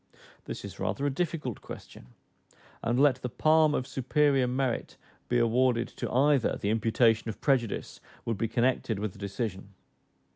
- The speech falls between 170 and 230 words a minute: No, average, 155 wpm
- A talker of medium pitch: No, low, 125 Hz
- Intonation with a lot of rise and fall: No, average, 3.3 semitones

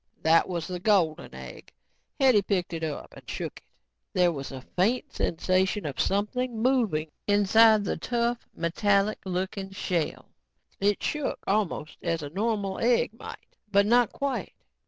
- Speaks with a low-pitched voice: No, high, 200 Hz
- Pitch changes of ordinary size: Yes, average, 4.6 semitones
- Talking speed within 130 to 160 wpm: Yes, average, 150 wpm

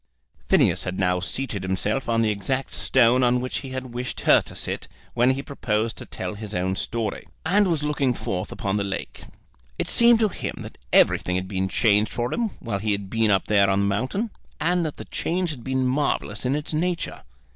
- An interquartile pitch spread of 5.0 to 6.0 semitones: Yes, average, 5.3 semitones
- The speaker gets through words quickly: Yes, fast, 210 wpm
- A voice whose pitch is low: Yes, low, 120 Hz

